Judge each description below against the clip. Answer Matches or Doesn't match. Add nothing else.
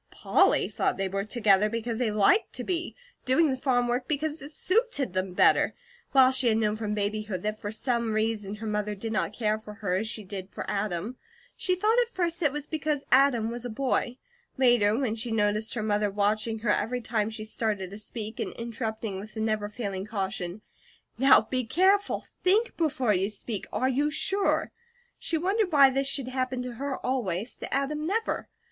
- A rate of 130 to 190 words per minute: Doesn't match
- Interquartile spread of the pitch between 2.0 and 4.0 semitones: Doesn't match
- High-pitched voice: Matches